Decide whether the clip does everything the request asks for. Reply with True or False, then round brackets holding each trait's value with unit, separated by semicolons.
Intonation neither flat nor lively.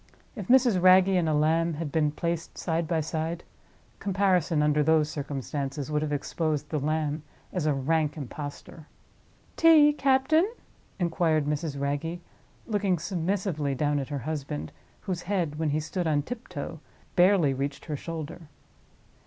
True (3.4 semitones)